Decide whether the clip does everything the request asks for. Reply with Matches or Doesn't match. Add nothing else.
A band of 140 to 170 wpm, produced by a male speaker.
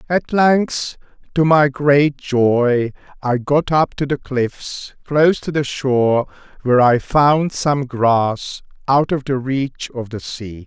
Matches